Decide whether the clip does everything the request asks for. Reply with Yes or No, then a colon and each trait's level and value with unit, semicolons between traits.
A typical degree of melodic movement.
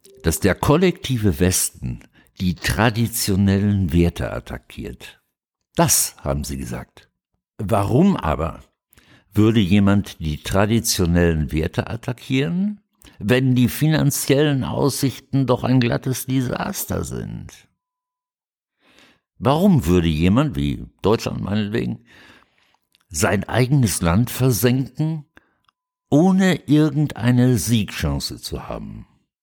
No: wide, 7.0 semitones